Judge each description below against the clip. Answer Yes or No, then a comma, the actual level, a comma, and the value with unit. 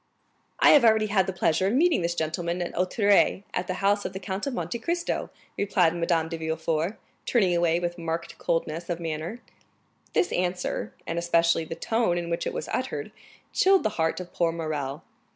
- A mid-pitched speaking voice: Yes, medium, 175 Hz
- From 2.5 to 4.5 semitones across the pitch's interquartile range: Yes, average, 3.4 semitones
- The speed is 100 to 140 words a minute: No, average, 190 wpm